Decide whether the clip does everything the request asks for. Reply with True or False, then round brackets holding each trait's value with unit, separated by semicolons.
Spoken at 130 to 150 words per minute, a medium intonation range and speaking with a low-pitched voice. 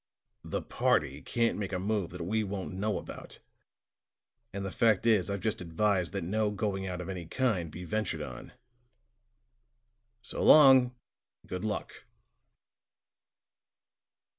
True (140 wpm; 3.1 semitones; 100 Hz)